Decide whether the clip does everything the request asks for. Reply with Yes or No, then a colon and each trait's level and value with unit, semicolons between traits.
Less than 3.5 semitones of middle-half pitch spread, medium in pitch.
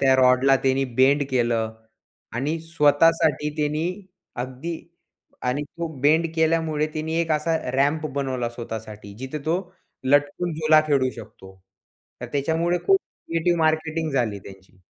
No: average, 3.8 semitones; medium, 145 Hz